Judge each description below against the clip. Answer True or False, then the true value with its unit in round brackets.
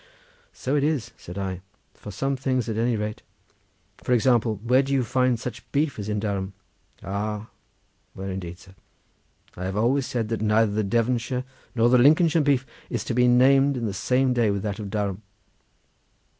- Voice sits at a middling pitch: False (115 Hz)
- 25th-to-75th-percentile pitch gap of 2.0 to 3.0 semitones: False (3.8 semitones)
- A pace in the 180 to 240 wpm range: True (185 wpm)